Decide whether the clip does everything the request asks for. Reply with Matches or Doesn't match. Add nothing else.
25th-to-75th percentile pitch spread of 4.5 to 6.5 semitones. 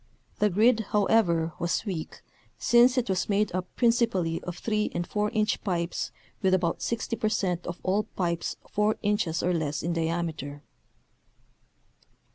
Doesn't match